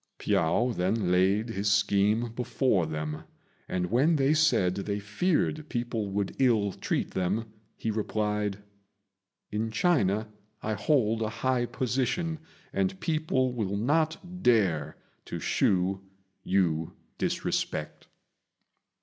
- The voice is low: Yes, low, 110 Hz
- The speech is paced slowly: Yes, slow, 115 wpm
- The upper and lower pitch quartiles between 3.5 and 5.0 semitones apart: Yes, average, 4.7 semitones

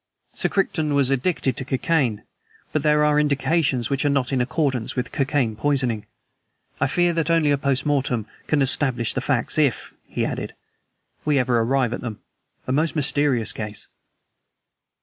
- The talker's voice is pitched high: No, low, 135 Hz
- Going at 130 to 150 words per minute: No, average, 165 wpm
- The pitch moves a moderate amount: Yes, average, 3.2 semitones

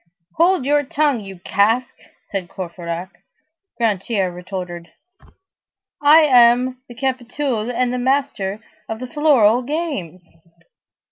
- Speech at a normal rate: No, slow, 110 wpm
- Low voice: No, high, 240 Hz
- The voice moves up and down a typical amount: No, wide, 6.2 semitones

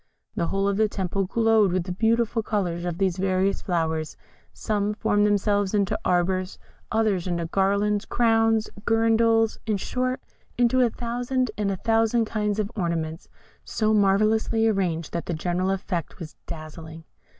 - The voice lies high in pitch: Yes, high, 200 Hz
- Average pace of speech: Yes, average, 150 wpm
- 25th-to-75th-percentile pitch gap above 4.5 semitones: No, average, 3.7 semitones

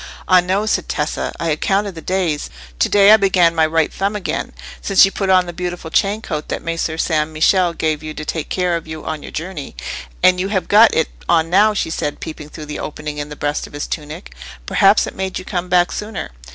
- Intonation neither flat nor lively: Yes, average, 3.7 semitones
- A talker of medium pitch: Yes, medium, 170 Hz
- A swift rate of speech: Yes, fast, 230 wpm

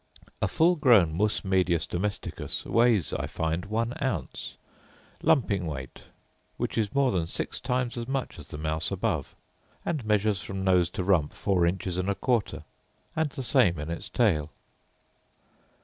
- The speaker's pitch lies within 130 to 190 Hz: No, low, 100 Hz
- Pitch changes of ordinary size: No, wide, 5.9 semitones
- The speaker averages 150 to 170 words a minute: Yes, average, 160 wpm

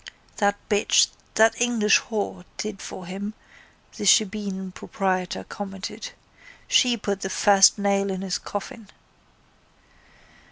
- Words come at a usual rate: No, slow, 115 wpm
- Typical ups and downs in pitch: No, narrow, 1.7 semitones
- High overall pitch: Yes, high, 200 Hz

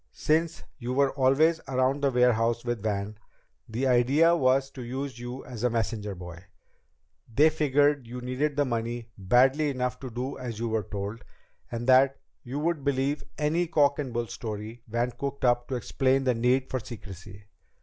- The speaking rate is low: No, average, 175 wpm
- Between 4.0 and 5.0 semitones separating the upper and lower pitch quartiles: No, average, 3.0 semitones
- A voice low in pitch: Yes, low, 125 Hz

